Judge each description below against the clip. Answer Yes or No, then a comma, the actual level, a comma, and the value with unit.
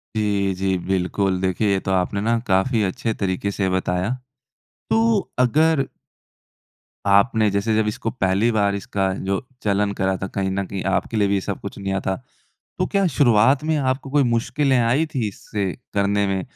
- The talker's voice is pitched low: Yes, low, 100 Hz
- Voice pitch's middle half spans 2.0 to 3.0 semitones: No, average, 3.6 semitones